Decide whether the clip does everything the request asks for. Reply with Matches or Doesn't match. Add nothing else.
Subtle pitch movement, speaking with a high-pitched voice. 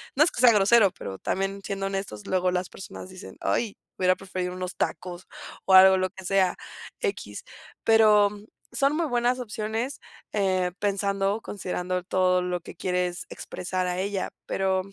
Matches